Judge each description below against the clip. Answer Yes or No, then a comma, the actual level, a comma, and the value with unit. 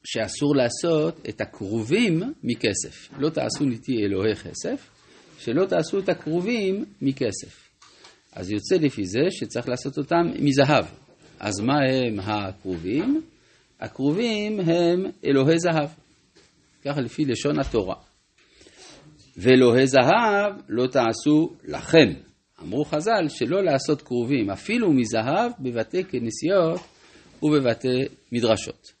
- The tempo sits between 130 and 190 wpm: No, average, 105 wpm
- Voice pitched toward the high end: No, low, 135 Hz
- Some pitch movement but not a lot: No, wide, 5.7 semitones